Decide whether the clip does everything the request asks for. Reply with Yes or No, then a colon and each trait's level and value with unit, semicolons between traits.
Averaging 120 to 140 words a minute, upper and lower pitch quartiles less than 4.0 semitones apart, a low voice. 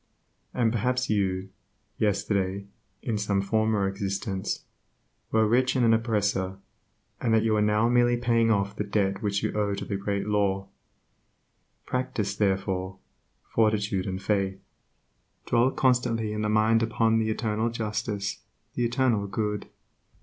Yes: slow, 135 wpm; narrow, 2.4 semitones; low, 105 Hz